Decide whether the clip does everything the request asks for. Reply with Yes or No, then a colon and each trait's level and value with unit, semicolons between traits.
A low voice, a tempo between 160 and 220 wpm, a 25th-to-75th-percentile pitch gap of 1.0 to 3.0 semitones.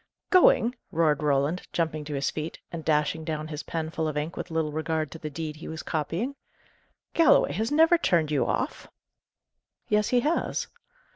No: medium, 160 Hz; average, 180 wpm; narrow, 2.5 semitones